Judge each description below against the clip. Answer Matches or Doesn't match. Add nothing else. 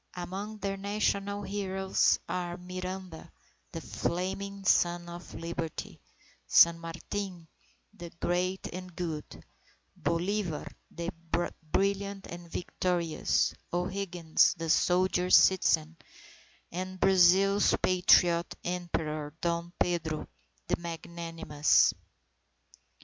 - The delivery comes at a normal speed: Doesn't match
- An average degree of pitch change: Doesn't match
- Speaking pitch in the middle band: Matches